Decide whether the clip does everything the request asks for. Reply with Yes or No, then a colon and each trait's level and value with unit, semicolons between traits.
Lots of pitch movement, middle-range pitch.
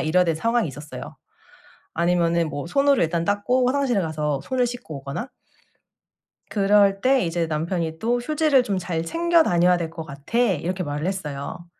Yes: wide, 6.9 semitones; medium, 180 Hz